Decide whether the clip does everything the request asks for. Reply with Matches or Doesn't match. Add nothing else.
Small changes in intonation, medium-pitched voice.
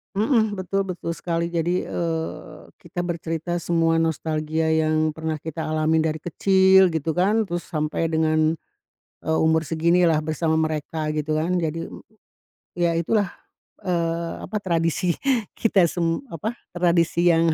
Matches